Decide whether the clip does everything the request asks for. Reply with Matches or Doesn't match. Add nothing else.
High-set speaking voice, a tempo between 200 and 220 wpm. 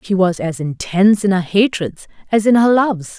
Matches